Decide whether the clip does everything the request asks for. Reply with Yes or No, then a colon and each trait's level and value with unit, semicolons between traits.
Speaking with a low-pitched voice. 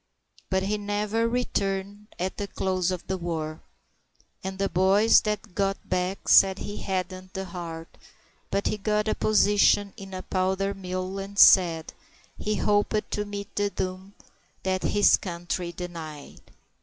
No: high, 190 Hz